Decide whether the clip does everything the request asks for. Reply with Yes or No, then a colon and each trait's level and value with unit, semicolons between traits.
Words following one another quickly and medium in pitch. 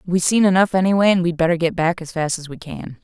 Yes: fast, 275 wpm; medium, 175 Hz